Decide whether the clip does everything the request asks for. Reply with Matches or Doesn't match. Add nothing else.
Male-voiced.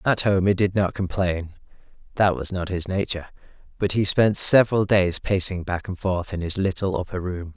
Matches